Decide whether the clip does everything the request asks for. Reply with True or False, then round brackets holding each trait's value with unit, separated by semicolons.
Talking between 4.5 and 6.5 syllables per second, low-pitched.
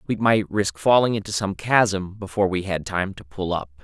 True (5.0 syllables/s; 95 Hz)